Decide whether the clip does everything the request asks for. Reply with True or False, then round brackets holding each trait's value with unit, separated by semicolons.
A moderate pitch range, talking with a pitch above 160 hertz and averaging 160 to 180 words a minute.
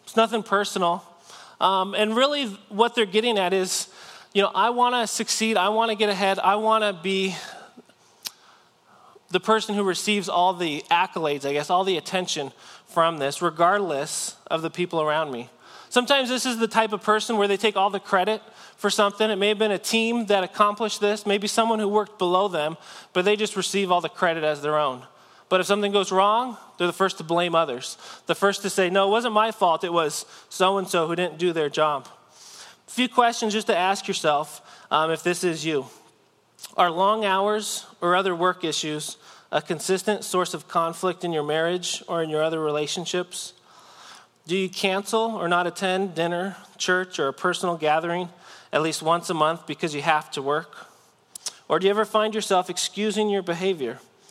False (3.8 semitones; 190 Hz; 200 wpm)